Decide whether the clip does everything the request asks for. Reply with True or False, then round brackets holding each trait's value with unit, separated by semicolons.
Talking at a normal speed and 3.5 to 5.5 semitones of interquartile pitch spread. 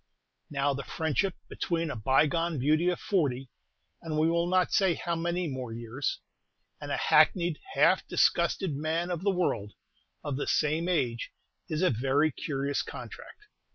True (155 wpm; 4.0 semitones)